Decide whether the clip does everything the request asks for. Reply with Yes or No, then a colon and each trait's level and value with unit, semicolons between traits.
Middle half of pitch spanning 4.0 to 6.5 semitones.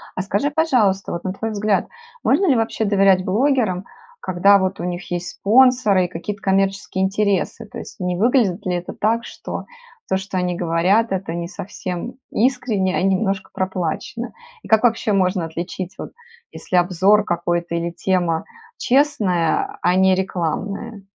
No: average, 3.2 semitones